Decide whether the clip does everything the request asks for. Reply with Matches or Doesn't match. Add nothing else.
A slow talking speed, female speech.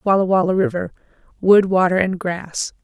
Matches